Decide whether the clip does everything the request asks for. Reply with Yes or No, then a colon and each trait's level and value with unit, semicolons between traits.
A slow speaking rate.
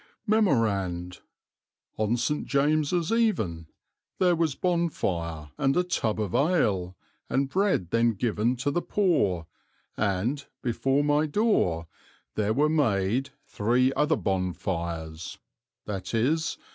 Yes: slow, 110 wpm